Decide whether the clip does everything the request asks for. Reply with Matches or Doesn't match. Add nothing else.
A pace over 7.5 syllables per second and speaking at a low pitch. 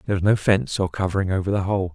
Matches